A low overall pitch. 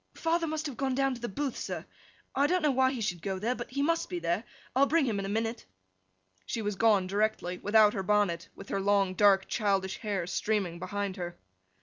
No: high, 210 Hz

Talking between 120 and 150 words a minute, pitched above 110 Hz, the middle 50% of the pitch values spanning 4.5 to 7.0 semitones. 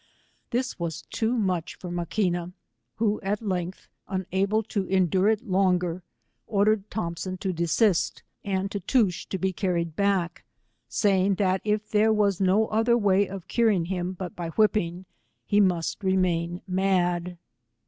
No: average, 140 wpm; high, 190 Hz; average, 2.8 semitones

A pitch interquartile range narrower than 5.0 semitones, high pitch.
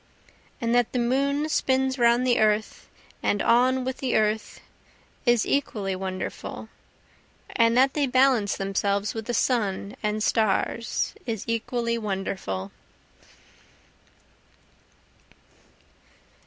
Yes: average, 3.5 semitones; high, 230 Hz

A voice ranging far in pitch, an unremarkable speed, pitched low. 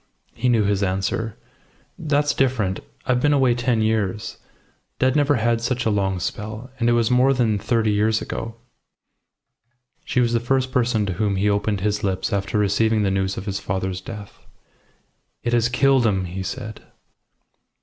No: average, 3.5 semitones; average, 170 wpm; low, 110 Hz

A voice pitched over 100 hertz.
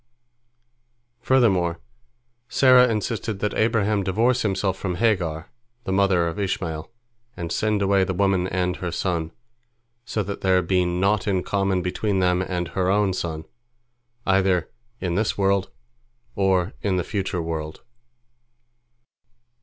No: very low, 95 Hz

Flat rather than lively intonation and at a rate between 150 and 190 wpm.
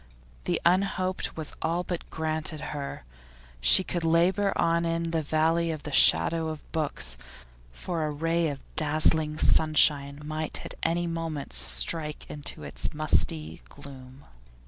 No: narrow, 2.3 semitones; average, 140 wpm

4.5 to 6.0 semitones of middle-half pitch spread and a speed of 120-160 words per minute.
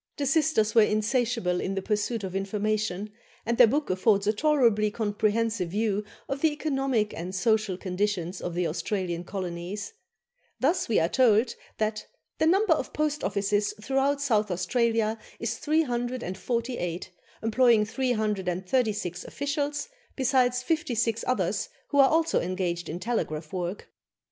Yes: average, 4.9 semitones; average, 140 wpm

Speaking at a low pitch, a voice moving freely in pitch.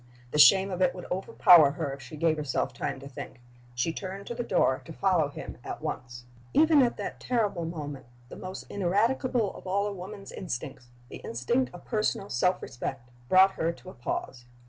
No: medium, 180 Hz; wide, 6.0 semitones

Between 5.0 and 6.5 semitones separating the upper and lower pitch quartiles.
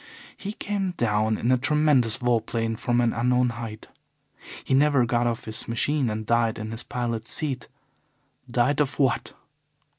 No: average, 2.8 semitones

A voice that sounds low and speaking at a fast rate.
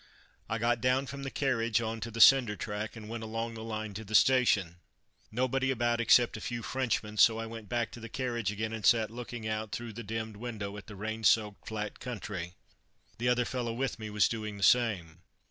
Yes: low, 115 Hz; fast, 215 wpm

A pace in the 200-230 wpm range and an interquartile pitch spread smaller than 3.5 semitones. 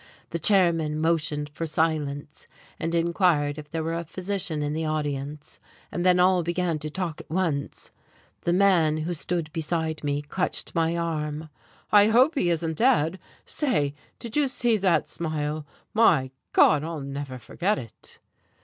No: average, 160 wpm; average, 3.1 semitones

